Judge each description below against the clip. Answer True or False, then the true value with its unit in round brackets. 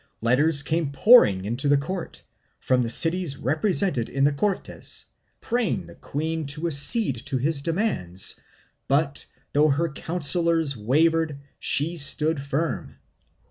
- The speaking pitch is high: False (150 Hz)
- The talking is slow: True (130 wpm)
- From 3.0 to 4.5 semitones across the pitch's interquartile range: True (3.3 semitones)